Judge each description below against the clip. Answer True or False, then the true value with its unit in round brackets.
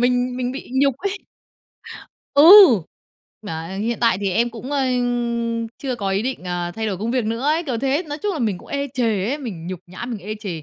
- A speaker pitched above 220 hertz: True (235 Hz)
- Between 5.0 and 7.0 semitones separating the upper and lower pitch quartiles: True (5.4 semitones)